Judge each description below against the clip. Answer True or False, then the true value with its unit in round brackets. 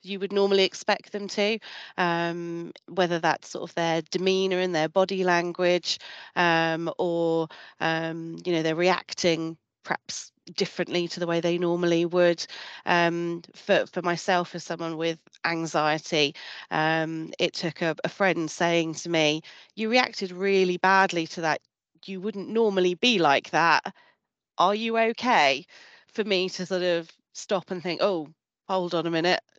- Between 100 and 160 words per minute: True (155 wpm)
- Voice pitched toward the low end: False (175 Hz)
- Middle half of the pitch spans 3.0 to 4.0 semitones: False (2.4 semitones)